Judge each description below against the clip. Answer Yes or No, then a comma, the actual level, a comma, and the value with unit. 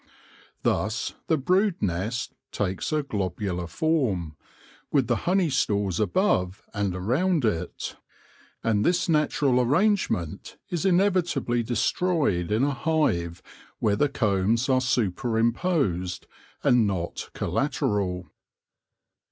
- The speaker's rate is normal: No, slow, 110 wpm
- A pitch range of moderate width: No, wide, 8.3 semitones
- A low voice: Yes, low, 120 Hz